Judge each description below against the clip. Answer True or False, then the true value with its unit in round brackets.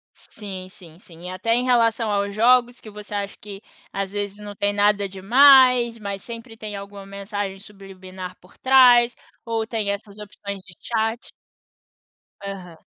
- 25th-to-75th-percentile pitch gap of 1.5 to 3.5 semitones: True (2.7 semitones)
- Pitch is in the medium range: False (205 Hz)